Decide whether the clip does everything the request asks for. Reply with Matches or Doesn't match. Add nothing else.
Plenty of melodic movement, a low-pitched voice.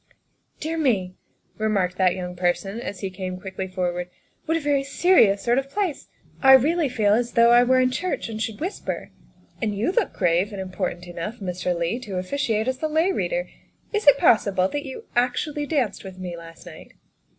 Doesn't match